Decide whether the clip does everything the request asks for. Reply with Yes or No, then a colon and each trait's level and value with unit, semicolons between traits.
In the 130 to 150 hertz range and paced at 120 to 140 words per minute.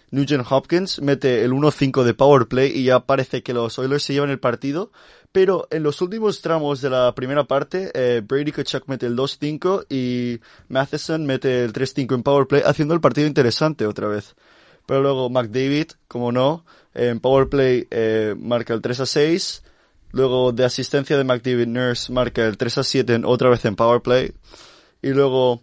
No: low, 135 Hz; average, 170 wpm